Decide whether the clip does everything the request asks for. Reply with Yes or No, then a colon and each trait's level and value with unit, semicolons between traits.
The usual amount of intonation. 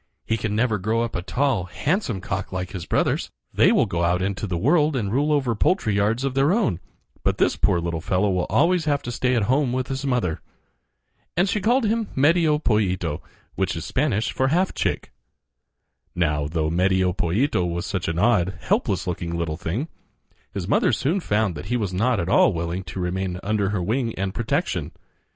No: wide, 6.9 semitones